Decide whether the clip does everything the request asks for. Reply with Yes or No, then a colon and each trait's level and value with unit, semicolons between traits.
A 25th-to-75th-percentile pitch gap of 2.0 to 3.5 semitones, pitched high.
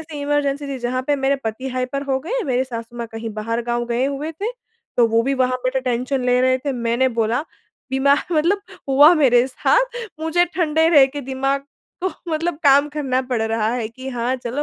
Yes: average, 3.1 semitones; very high, 265 Hz